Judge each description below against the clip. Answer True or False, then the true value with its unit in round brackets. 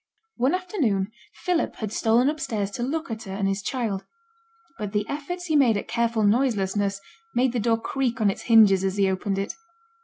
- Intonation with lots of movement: False (4.7 semitones)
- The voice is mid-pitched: False (225 Hz)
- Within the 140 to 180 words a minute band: False (190 wpm)